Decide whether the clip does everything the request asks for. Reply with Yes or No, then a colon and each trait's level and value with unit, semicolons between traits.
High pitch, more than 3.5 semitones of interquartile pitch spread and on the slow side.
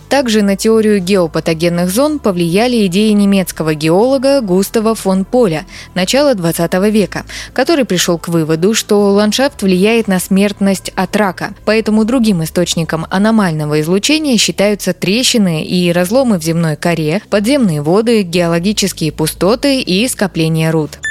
No: high, 195 Hz; average, 4.2 semitones; average, 130 wpm